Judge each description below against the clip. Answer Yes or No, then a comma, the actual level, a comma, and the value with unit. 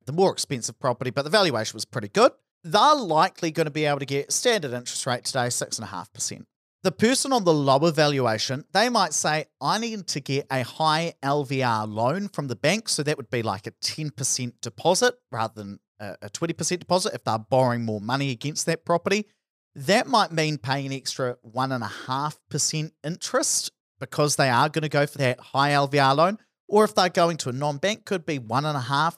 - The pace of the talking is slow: No, average, 195 wpm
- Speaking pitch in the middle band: Yes, medium, 145 Hz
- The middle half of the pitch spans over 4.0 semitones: Yes, average, 4.8 semitones